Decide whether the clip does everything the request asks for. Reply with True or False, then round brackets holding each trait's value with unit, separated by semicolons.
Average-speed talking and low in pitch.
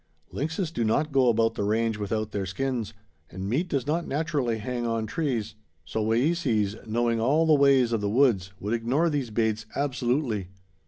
True (175 wpm; 120 Hz)